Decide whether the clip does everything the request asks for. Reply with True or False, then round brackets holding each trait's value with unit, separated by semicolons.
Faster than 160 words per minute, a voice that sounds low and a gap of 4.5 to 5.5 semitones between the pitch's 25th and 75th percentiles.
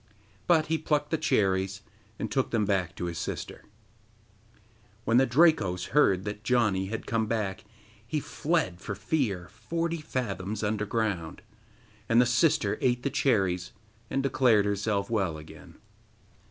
False (140 wpm; 110 Hz; 5.0 semitones)